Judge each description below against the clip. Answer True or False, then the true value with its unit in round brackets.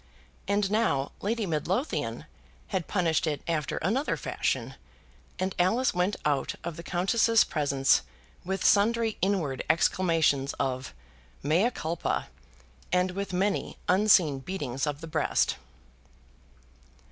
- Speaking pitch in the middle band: True (180 Hz)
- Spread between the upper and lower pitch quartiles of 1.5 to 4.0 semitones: False (5.0 semitones)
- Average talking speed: False (115 wpm)